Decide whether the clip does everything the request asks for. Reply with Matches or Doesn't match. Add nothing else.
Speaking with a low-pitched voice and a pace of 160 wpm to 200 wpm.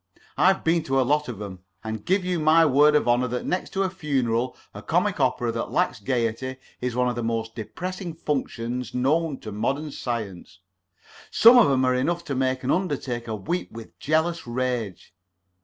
Matches